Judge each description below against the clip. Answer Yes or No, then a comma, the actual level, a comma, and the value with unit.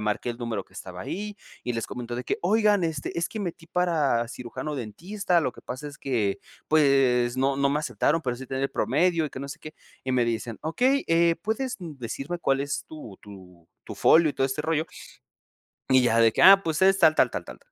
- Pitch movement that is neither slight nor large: No, wide, 5.7 semitones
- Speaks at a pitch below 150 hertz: Yes, medium, 140 Hz